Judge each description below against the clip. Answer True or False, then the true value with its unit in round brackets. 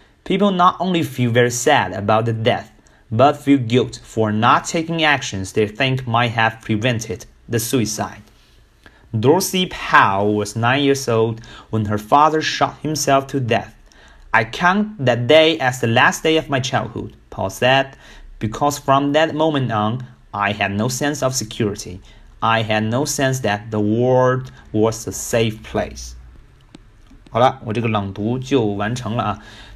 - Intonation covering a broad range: False (4.3 semitones)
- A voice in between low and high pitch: False (120 Hz)